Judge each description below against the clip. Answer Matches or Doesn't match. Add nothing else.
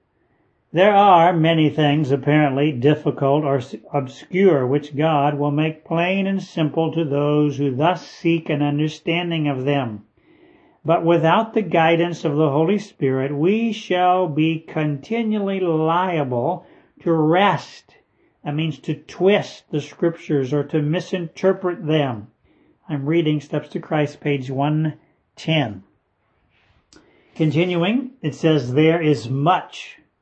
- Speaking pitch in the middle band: Matches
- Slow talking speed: Matches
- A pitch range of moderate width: Matches